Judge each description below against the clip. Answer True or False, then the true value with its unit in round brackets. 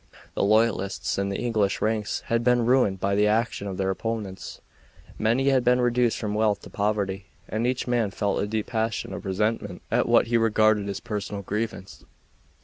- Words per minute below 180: False (185 wpm)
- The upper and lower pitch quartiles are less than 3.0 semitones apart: True (2.6 semitones)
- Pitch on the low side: True (110 Hz)